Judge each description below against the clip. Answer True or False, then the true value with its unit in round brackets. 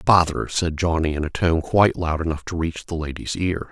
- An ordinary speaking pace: False (225 wpm)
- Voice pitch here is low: True (85 Hz)